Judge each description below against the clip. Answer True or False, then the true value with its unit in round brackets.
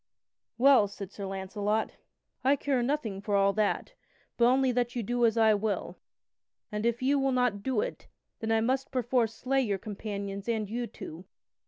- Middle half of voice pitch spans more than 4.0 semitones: False (3.6 semitones)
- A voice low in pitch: False (225 Hz)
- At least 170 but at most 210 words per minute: True (180 wpm)